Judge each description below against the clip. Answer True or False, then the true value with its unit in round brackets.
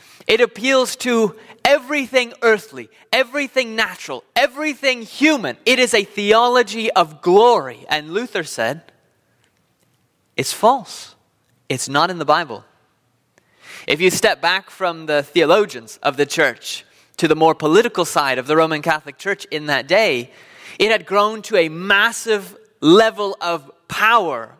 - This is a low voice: False (215 Hz)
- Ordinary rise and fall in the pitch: False (7.5 semitones)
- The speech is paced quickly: False (140 wpm)